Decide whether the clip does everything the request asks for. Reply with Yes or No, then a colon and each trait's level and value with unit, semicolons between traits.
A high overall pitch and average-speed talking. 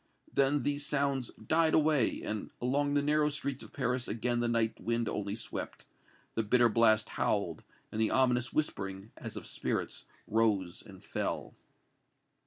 No: low, 120 Hz; average, 155 wpm